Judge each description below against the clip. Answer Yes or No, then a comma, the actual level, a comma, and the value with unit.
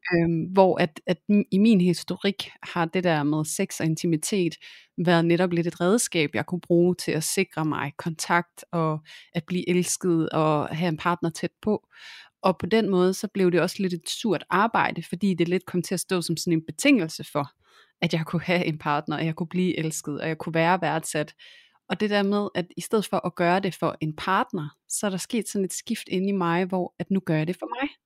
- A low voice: No, medium, 175 Hz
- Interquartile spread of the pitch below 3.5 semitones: Yes, average, 2.7 semitones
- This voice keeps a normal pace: No, fast, 235 wpm